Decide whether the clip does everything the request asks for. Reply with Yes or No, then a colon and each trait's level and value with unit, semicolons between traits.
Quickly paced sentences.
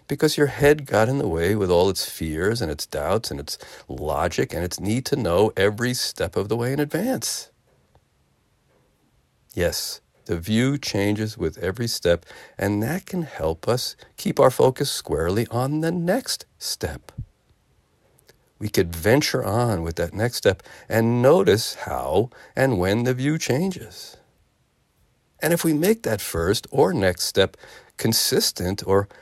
No: average, 155 wpm